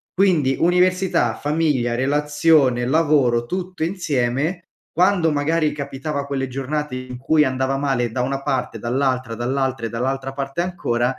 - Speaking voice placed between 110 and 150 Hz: Yes, medium, 140 Hz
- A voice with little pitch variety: No, average, 3.7 semitones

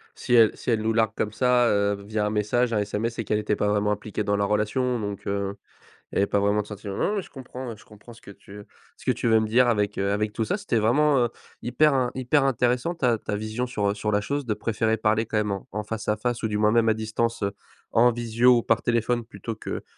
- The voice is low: Yes, low, 110 Hz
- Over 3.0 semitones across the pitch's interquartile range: No, narrow, 2.5 semitones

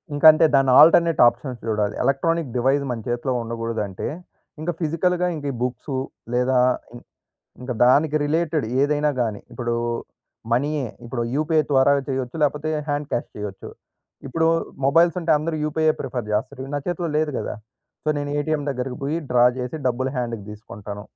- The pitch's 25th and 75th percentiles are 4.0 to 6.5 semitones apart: Yes, average, 4.3 semitones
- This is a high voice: No, low, 135 Hz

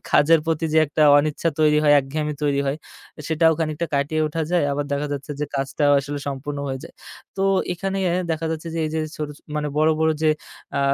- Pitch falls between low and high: Yes, medium, 150 Hz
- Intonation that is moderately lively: No, narrow, 1.9 semitones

